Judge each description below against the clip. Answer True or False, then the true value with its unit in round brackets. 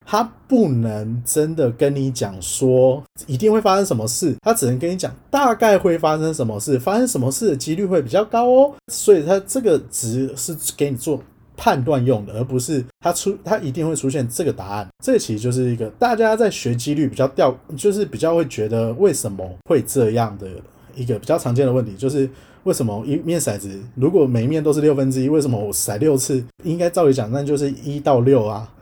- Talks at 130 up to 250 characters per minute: False (315 characters per minute)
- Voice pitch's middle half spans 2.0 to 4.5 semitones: False (5.3 semitones)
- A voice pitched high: False (140 Hz)